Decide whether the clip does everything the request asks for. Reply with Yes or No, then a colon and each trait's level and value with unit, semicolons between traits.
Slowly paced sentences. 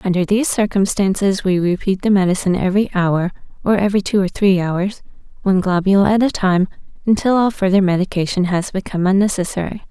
No: average, 165 wpm